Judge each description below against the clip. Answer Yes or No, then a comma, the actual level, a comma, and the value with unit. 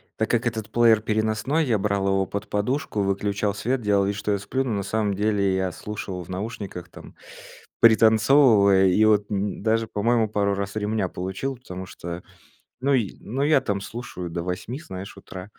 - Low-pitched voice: Yes, low, 105 Hz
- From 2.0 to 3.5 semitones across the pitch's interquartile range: Yes, narrow, 2.5 semitones